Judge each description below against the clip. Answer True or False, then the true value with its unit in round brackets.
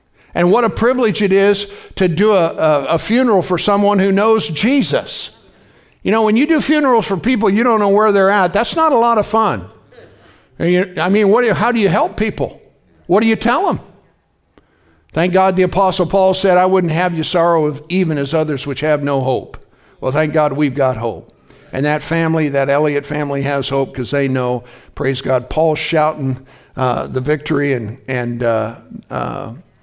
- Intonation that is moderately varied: False (6.6 semitones)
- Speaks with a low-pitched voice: False (165 Hz)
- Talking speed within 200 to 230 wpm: True (205 wpm)